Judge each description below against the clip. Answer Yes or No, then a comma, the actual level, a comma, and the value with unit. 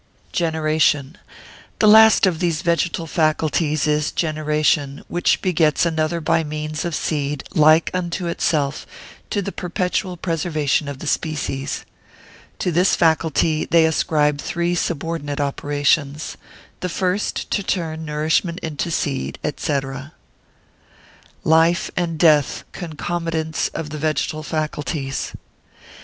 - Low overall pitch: No, medium, 160 Hz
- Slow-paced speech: Yes, slow, 115 wpm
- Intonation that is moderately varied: No, narrow, 2.2 semitones